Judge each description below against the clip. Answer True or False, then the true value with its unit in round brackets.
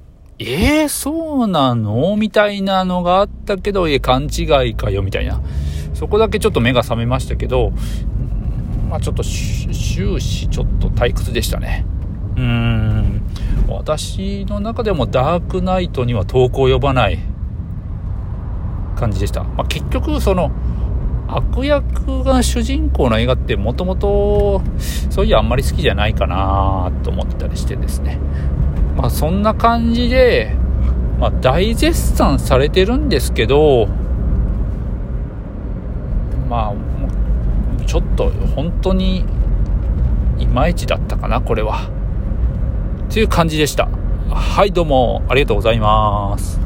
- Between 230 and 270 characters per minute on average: True (260 characters per minute)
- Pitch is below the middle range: True (95 Hz)